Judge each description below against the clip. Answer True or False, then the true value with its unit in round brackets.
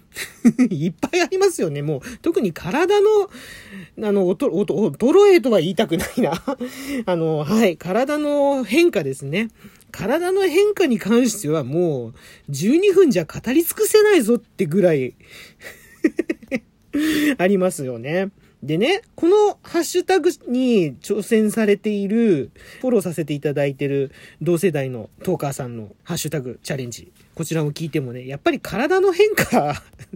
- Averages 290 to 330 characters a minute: True (295 characters per minute)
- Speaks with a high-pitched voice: True (210 Hz)